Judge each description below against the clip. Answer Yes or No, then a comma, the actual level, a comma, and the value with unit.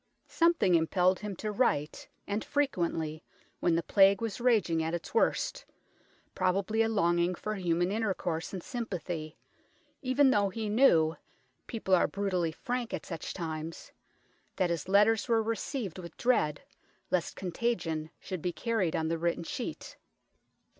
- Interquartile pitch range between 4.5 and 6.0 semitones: Yes, average, 4.9 semitones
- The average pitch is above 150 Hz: Yes, medium, 185 Hz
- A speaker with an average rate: Yes, average, 150 wpm